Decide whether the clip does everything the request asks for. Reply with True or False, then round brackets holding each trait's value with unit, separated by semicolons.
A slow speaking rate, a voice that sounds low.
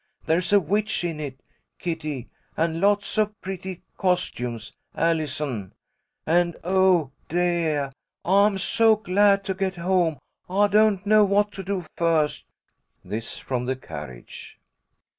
False (125 wpm; 175 Hz)